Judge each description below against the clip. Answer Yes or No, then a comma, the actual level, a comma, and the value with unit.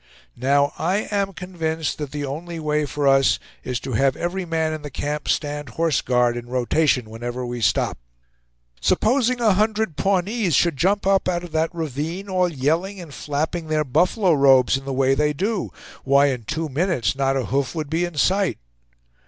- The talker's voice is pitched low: No, medium, 155 Hz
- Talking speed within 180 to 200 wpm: Yes, average, 185 wpm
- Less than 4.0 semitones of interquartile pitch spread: No, average, 4.6 semitones